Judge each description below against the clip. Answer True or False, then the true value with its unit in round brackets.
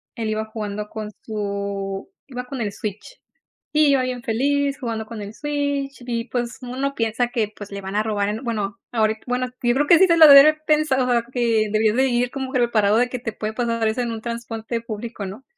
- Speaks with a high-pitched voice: True (235 Hz)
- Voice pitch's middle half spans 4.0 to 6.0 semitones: False (3.3 semitones)